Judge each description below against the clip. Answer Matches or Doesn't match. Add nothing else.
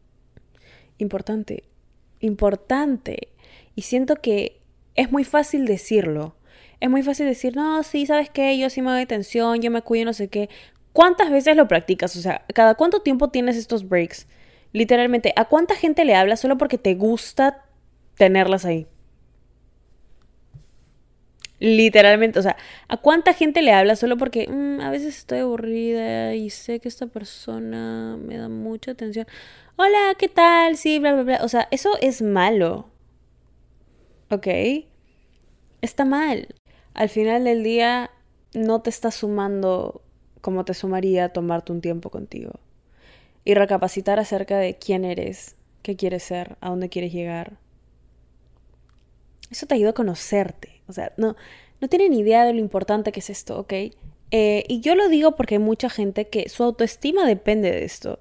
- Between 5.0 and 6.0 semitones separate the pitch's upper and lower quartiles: Matches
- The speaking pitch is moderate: Doesn't match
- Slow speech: Doesn't match